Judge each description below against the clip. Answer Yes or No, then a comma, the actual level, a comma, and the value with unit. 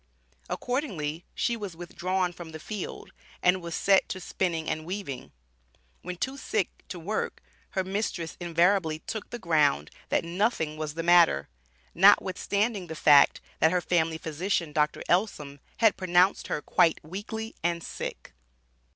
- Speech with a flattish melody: No, average, 3.6 semitones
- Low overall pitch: No, medium, 175 Hz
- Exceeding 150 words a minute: No, average, 145 wpm